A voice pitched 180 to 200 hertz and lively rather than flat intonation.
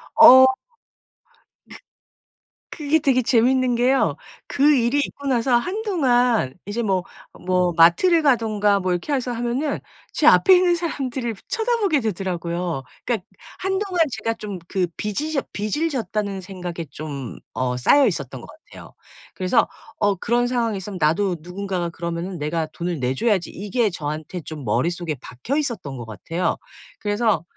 No: high, 210 Hz; wide, 7.1 semitones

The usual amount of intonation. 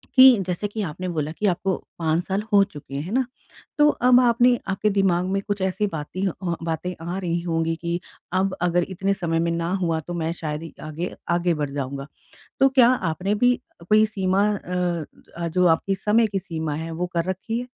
Yes: average, 3.5 semitones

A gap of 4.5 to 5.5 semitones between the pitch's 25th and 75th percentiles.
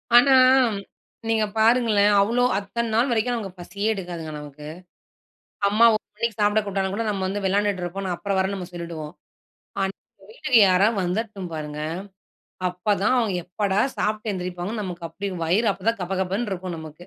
No: average, 3.3 semitones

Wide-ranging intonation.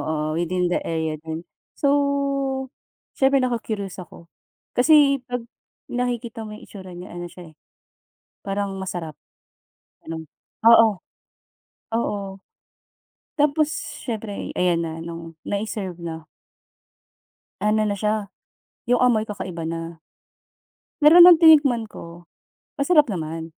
Yes: wide, 6.7 semitones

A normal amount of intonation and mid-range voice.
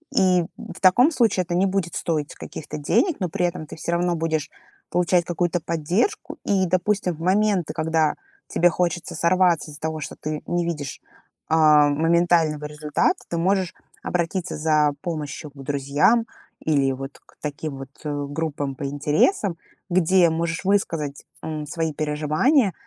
Yes: average, 3.1 semitones; medium, 165 Hz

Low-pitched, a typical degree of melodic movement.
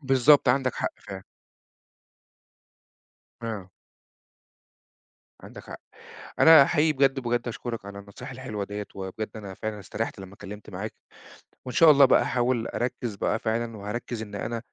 Yes: low, 115 Hz; average, 3.9 semitones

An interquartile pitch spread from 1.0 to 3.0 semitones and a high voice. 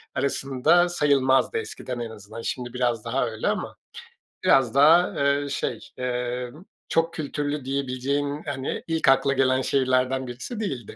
No: narrow, 2.4 semitones; low, 135 Hz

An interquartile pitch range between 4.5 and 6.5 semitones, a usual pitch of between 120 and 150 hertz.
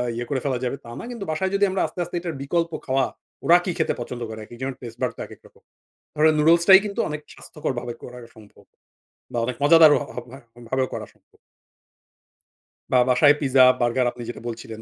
Yes: average, 5.3 semitones; low, 135 Hz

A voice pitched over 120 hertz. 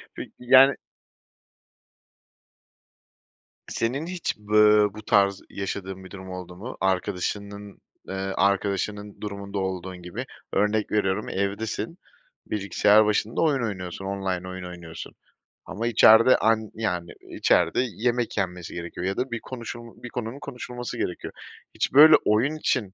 No: low, 105 Hz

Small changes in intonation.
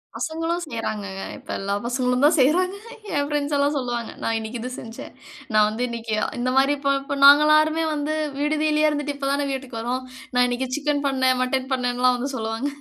No: average, 3.3 semitones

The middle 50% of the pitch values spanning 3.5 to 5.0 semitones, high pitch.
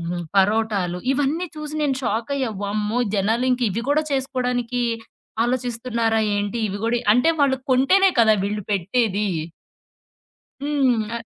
Yes: average, 3.9 semitones; high, 235 Hz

